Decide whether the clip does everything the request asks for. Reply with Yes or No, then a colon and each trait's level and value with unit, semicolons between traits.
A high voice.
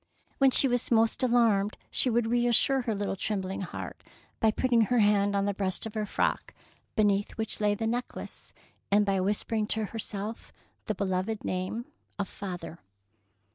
Yes: high, 210 Hz